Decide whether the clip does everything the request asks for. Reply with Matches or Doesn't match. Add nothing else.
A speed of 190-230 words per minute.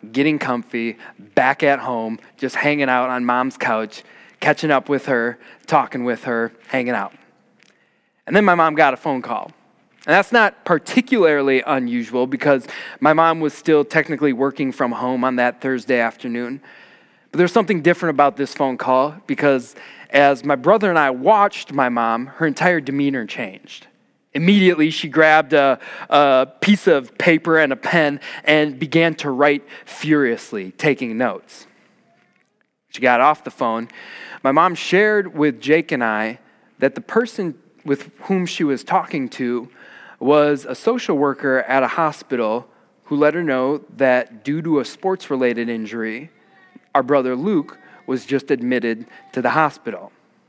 Doesn't match